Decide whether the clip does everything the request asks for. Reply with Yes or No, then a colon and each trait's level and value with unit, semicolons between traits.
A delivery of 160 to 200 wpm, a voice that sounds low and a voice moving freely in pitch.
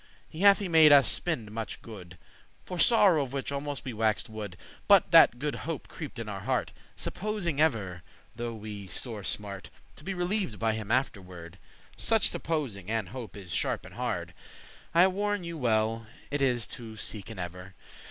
Yes: average, 180 wpm; low, 120 Hz; wide, 7.3 semitones